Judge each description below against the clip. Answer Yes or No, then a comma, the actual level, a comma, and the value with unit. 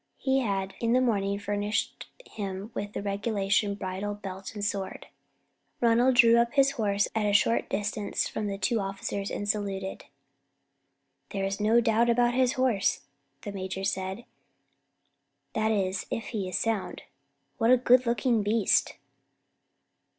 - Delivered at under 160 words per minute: Yes, average, 145 wpm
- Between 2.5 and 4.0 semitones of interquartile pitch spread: Yes, average, 2.9 semitones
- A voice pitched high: Yes, high, 205 Hz